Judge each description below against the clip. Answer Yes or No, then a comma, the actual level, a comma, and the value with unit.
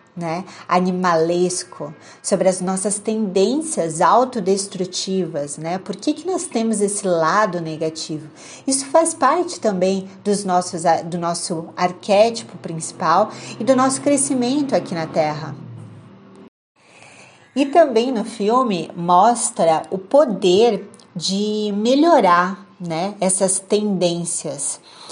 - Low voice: No, high, 190 Hz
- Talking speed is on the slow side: Yes, slow, 110 wpm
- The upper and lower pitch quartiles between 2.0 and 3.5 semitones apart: No, average, 4.5 semitones